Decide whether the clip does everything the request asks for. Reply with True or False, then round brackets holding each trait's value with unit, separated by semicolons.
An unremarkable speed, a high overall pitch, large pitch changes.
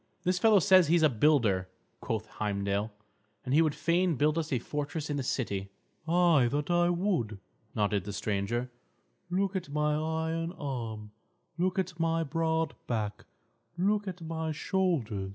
False (160 wpm; 155 Hz; 7.2 semitones)